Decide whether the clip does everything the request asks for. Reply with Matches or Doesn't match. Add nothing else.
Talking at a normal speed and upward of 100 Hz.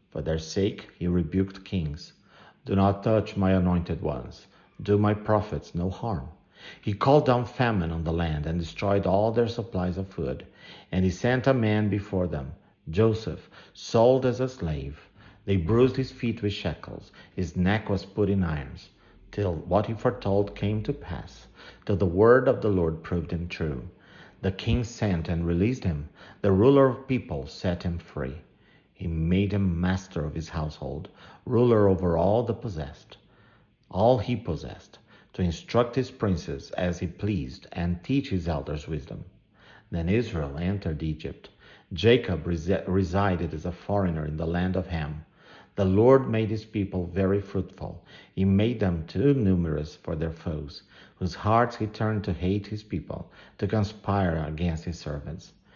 Doesn't match